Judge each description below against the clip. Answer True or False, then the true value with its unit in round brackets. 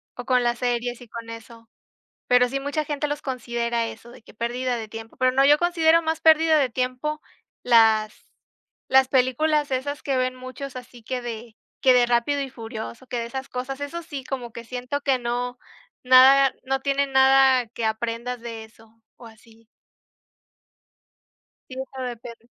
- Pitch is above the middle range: True (250 Hz)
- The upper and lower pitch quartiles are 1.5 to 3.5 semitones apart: True (2.5 semitones)